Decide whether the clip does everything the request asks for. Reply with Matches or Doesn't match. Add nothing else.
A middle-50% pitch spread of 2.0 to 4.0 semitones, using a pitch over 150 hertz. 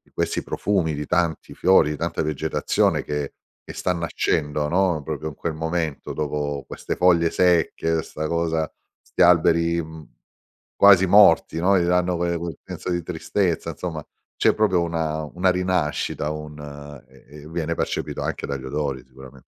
Doesn't match